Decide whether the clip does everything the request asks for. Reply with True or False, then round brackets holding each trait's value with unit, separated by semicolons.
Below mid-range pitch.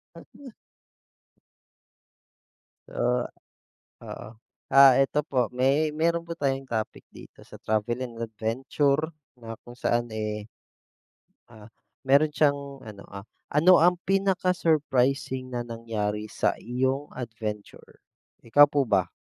True (130 Hz)